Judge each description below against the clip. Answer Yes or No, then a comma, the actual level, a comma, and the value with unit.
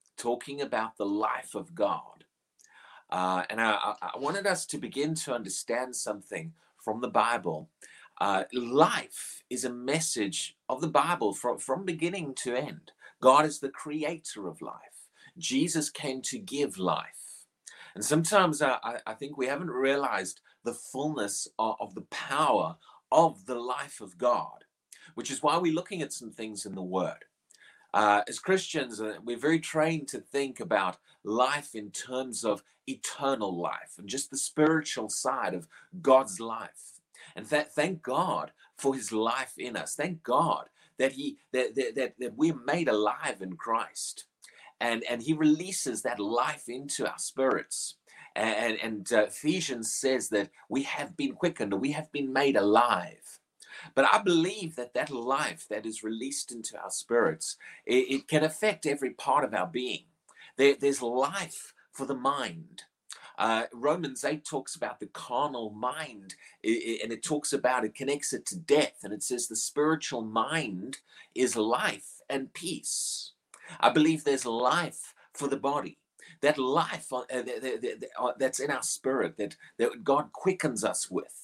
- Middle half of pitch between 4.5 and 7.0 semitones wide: Yes, average, 4.9 semitones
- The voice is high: No, low, 135 Hz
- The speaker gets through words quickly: No, average, 160 wpm